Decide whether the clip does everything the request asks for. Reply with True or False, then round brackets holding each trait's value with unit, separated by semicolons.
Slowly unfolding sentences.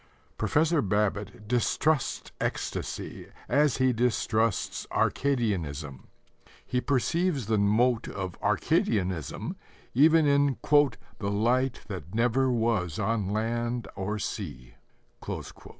True (95 wpm)